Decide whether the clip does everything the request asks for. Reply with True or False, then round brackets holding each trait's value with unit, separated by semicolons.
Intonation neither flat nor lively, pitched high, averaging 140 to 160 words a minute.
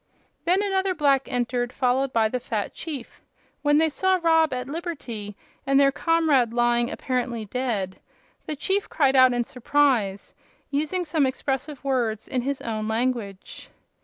True (4.0 semitones; 260 Hz; 150 wpm)